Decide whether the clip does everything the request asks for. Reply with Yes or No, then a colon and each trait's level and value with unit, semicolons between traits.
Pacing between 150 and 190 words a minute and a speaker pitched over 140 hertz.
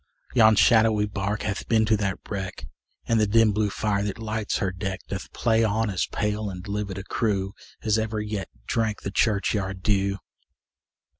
No: average, 175 wpm; low, 105 Hz